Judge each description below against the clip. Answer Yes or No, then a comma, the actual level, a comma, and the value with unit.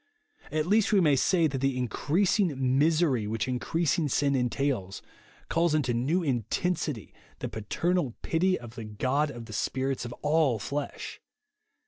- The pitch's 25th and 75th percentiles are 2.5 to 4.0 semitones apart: No, average, 5.0 semitones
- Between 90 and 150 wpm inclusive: Yes, average, 145 wpm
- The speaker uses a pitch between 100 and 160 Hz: Yes, medium, 140 Hz